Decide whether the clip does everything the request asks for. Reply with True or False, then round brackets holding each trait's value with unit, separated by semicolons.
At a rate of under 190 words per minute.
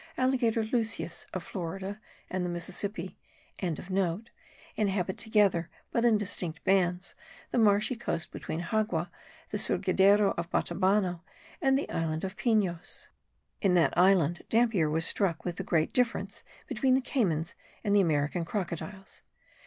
True (135 wpm)